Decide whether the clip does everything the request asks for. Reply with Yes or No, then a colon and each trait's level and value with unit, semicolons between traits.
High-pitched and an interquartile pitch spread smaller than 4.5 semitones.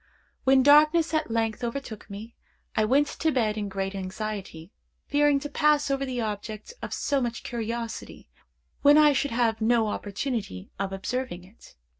No: high, 235 Hz; average, 4.9 semitones